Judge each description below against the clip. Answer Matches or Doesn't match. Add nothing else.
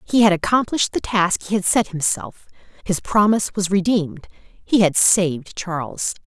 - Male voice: Doesn't match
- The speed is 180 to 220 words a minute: Doesn't match